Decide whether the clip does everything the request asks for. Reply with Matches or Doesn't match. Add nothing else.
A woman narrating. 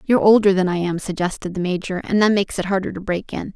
Matches